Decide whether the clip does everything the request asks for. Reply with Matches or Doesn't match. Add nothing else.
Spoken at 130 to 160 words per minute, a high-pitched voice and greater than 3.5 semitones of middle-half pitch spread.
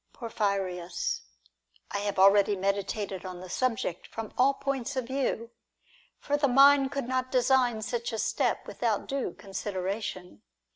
Matches